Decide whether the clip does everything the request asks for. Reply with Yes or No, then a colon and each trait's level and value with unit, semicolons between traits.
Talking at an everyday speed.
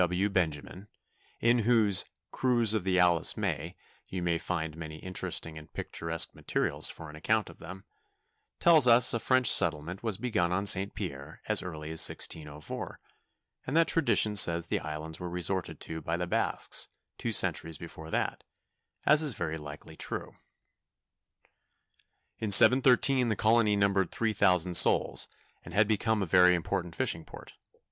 Yes: average, 160 wpm